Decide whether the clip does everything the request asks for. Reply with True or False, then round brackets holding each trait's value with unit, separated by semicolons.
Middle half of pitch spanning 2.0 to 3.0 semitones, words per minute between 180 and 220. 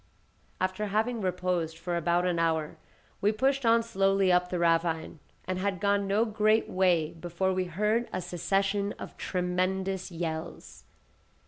False (2.7 semitones; 145 wpm)